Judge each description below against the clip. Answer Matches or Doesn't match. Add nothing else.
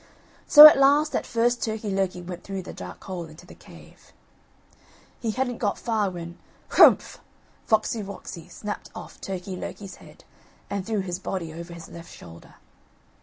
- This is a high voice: Matches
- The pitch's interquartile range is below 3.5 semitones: Doesn't match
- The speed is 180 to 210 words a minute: Doesn't match